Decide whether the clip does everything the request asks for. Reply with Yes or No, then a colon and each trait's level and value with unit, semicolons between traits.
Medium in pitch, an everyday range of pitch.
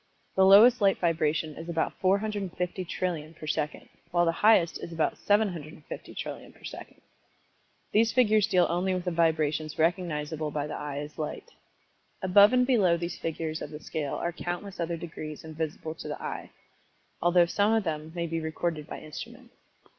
Yes: medium, 170 Hz; average, 3.5 semitones